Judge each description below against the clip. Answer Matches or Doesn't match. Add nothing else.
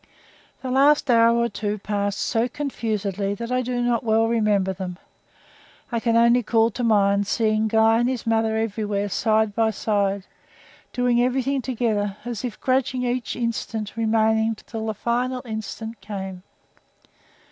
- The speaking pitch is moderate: Doesn't match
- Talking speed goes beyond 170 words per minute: Doesn't match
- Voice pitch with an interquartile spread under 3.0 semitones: Matches